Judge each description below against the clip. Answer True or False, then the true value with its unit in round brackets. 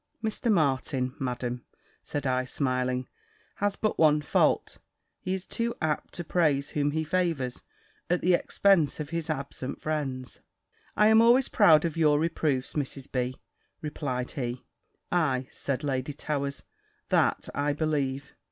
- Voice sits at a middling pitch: True (145 Hz)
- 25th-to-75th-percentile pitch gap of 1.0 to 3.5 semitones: False (4.2 semitones)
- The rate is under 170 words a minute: True (145 wpm)